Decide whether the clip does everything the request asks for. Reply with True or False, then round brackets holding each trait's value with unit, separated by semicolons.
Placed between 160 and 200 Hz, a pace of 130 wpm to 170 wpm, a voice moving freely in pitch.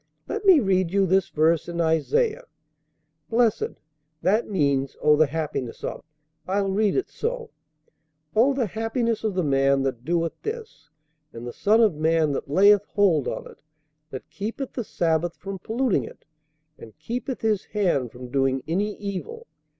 True (190 Hz; 160 wpm; 6.6 semitones)